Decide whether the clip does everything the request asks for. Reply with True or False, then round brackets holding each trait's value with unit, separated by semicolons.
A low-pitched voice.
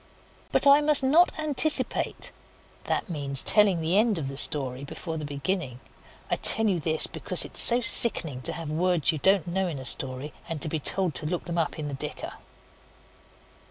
False (165 Hz)